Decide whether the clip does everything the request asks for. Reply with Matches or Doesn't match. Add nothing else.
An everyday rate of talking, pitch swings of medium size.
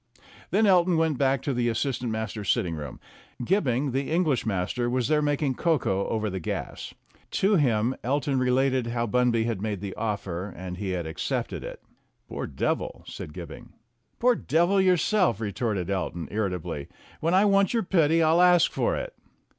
Doesn't match